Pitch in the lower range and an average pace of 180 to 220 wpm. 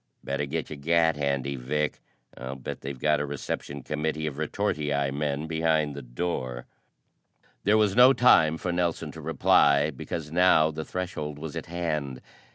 No: very low, 75 Hz; average, 165 wpm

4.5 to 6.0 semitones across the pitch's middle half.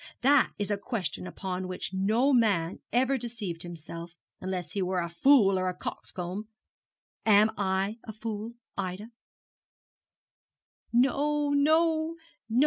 Yes: average, 5.0 semitones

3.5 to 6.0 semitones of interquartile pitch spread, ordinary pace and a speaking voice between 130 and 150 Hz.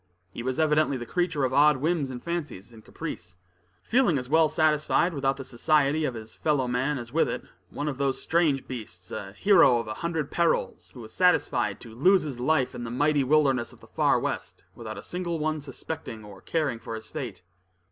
No: average, 4.4 semitones; fast, 210 wpm; medium, 140 Hz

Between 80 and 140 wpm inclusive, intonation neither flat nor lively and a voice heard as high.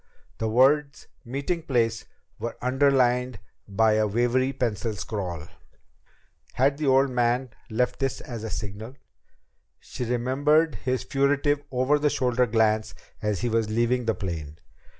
No: slow, 135 wpm; average, 3.3 semitones; low, 125 Hz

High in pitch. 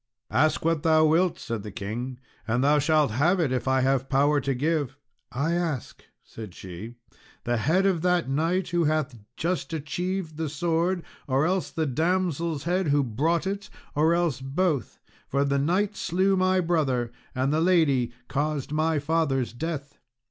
No: medium, 155 Hz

